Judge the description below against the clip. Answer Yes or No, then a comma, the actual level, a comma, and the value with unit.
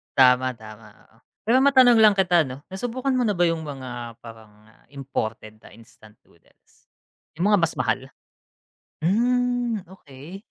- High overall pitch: No, medium, 160 Hz